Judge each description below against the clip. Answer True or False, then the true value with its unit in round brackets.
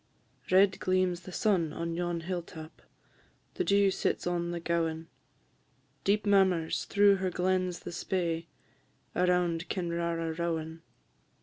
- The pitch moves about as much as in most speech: False (1.9 semitones)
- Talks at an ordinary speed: False (130 wpm)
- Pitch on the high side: False (175 Hz)